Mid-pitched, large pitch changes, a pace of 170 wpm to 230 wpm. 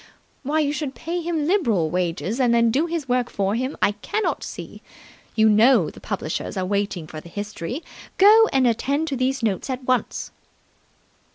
No: very high, 250 Hz; wide, 6.2 semitones; average, 180 wpm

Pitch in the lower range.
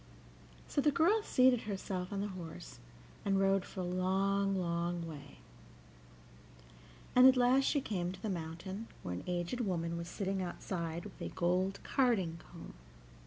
No: high, 190 Hz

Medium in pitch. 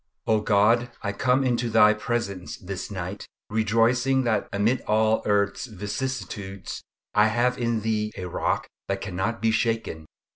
No: low, 110 Hz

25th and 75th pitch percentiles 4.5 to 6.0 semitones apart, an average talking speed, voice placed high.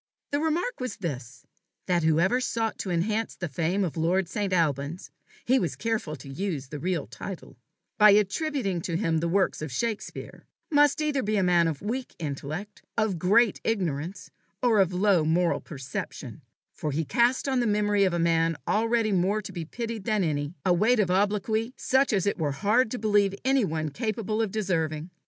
Yes: average, 5.1 semitones; average, 185 wpm; high, 195 Hz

